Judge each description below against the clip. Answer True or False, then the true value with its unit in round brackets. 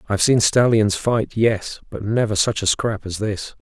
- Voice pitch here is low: True (105 Hz)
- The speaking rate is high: False (195 wpm)